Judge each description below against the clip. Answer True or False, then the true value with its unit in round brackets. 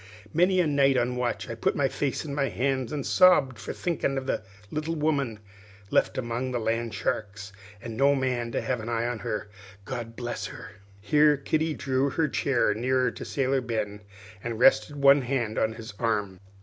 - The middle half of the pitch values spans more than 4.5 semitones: False (3.5 semitones)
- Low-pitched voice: True (130 Hz)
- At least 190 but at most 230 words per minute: True (195 wpm)